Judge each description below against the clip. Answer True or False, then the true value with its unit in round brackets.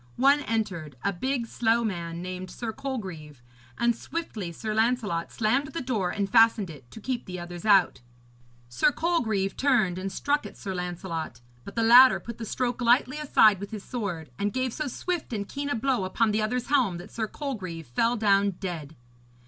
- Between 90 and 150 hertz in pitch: False (215 Hz)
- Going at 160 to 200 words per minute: True (190 wpm)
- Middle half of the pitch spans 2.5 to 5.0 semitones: False (5.4 semitones)